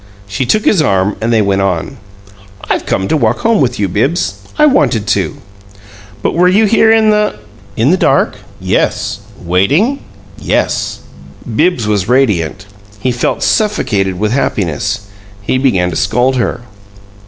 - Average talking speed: Yes, average, 155 wpm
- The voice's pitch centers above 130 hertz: No, low, 120 Hz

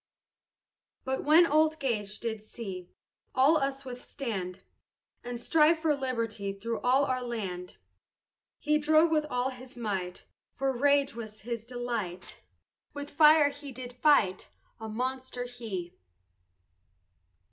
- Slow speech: Yes, slow, 125 wpm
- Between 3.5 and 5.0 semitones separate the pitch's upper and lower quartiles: Yes, average, 4.6 semitones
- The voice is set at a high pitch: Yes, very high, 250 Hz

